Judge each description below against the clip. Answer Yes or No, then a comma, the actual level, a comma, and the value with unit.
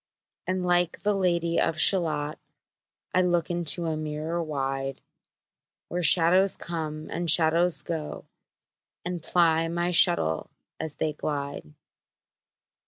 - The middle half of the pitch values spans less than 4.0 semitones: Yes, narrow, 2.4 semitones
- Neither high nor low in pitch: Yes, medium, 165 Hz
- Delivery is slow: Yes, slow, 115 wpm